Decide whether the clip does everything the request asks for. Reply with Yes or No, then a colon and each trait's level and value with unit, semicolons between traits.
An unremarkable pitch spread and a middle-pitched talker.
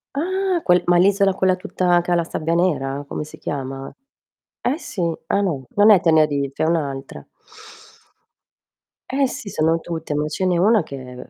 Yes: average, 4.9 semitones; medium, 170 Hz